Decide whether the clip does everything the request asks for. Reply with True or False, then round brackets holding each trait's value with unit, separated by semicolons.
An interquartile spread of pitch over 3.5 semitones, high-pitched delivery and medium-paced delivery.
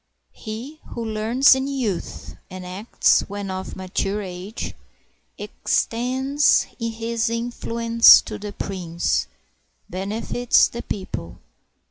False (3.9 semitones; 220 Hz; 100 wpm)